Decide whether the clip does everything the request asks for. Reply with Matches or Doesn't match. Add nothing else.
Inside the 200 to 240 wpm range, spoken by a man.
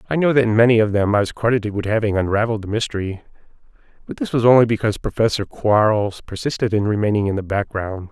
Matches